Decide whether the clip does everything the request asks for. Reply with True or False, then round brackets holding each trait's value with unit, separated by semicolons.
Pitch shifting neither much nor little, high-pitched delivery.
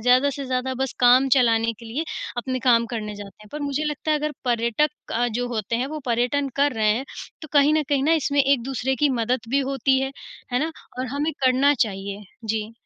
True (3.5 semitones; 255 Hz)